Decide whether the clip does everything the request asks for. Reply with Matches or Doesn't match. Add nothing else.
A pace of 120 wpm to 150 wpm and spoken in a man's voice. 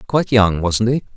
Doesn't match